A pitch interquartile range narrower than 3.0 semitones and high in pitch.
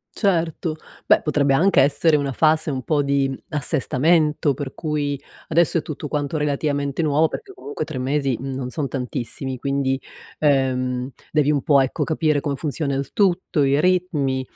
No: narrow, 2.4 semitones; medium, 145 Hz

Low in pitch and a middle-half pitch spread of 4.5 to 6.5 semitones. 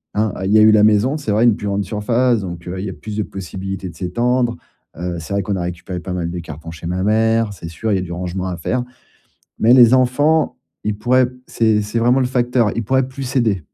Yes: low, 105 Hz; average, 4.8 semitones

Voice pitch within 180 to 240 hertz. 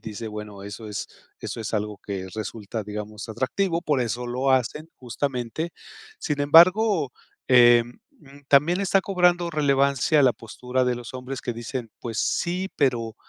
No: low, 125 Hz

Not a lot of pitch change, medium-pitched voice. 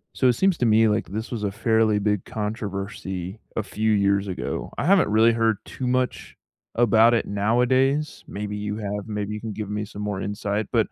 No: narrow, 2.0 semitones; low, 105 Hz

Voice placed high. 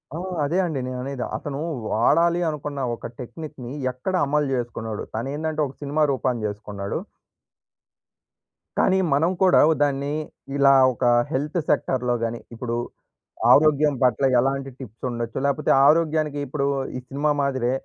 No: medium, 140 Hz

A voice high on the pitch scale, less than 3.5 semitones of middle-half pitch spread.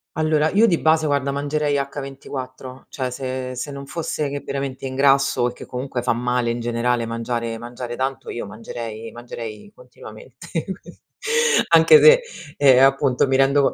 No: low, 130 Hz; average, 2.7 semitones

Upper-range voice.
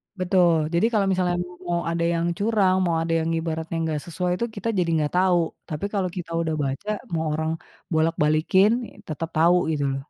No: medium, 170 Hz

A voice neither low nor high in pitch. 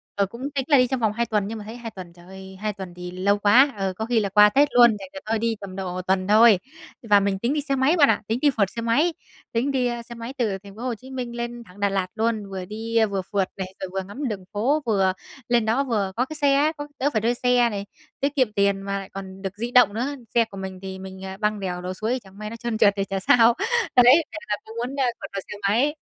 No: high, 220 Hz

